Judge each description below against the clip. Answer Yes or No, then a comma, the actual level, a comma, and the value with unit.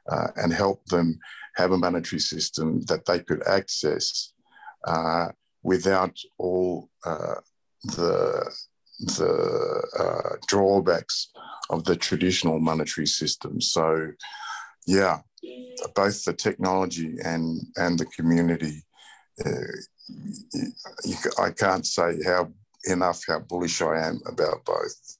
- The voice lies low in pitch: Yes, very low, 95 Hz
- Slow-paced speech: Yes, slow, 110 wpm